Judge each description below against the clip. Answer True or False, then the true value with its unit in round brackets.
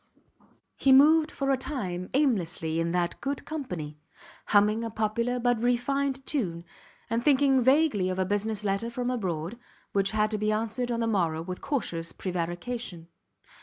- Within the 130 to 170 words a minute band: True (160 wpm)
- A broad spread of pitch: True (6.0 semitones)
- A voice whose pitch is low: False (220 Hz)